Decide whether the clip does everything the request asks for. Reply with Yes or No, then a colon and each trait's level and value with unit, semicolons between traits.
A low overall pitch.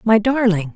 No: high, 215 Hz